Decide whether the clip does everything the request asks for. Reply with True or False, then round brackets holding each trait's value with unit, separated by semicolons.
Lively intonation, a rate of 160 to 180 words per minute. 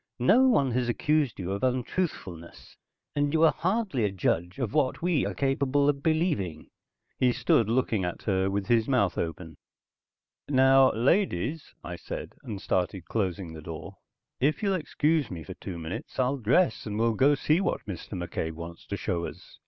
True (7.9 semitones; 175 wpm)